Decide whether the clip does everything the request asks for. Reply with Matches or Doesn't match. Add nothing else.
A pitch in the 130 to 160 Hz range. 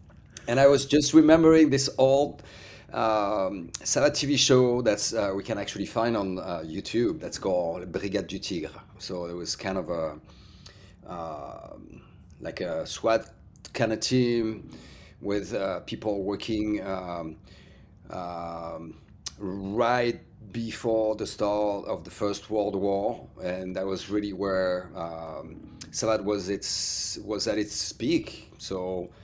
Doesn't match